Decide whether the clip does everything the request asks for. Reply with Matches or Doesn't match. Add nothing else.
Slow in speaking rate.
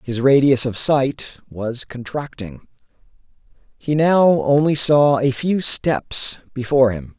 Matches